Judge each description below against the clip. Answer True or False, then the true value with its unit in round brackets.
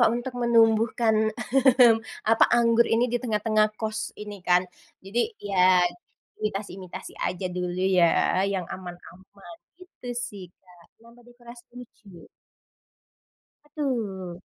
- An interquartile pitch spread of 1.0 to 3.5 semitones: False (4.2 semitones)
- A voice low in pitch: False (215 Hz)